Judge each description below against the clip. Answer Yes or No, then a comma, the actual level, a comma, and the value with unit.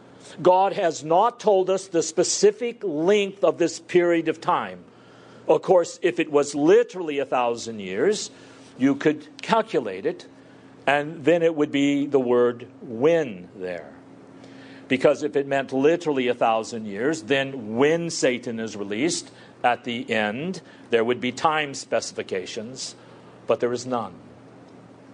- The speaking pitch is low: No, medium, 145 Hz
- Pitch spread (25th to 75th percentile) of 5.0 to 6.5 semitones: Yes, wide, 5.5 semitones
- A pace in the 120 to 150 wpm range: Yes, average, 145 wpm